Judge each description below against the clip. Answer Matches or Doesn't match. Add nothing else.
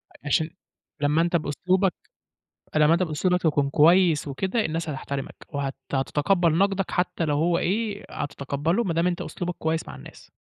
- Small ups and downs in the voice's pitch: Doesn't match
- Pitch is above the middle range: Doesn't match